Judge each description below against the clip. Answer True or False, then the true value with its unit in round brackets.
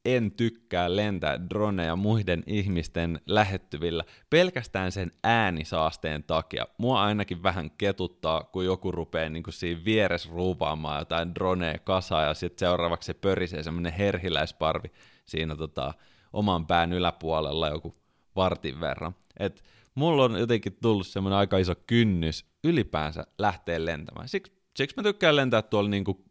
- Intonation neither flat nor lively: True (4.0 semitones)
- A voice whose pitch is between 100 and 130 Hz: False (90 Hz)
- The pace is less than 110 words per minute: False (135 wpm)